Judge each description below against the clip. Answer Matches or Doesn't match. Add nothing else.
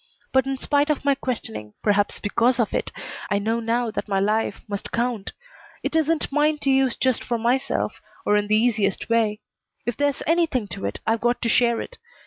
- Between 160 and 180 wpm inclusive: Doesn't match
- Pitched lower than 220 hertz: Doesn't match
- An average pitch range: Matches